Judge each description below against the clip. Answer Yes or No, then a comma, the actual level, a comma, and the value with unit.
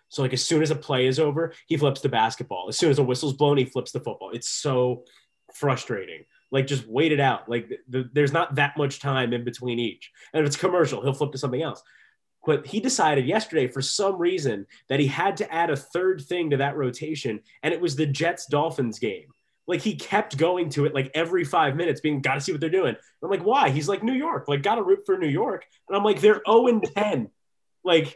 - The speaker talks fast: Yes, fast, 240 wpm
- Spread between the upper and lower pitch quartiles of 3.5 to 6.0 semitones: Yes, average, 4.4 semitones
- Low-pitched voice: No, medium, 145 Hz